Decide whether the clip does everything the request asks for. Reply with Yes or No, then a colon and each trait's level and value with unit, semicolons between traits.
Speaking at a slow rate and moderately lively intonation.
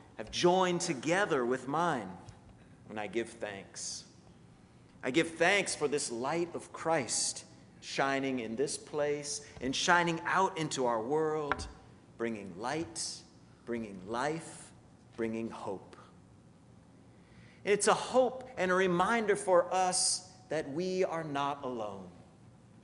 No: slow, 120 wpm; wide, 6.8 semitones